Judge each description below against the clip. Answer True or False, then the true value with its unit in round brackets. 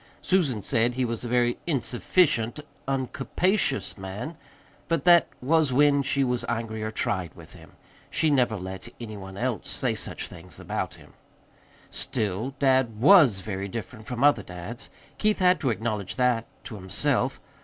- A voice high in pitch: False (120 Hz)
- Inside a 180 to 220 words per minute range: False (155 wpm)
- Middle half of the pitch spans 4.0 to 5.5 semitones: True (4.4 semitones)